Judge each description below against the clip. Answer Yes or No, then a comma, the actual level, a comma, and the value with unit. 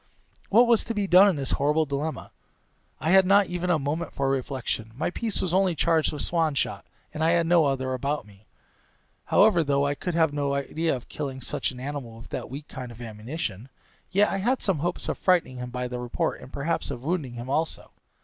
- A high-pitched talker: No, medium, 150 Hz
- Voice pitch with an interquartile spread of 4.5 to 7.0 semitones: Yes, average, 5.1 semitones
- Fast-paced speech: Yes, fast, 220 wpm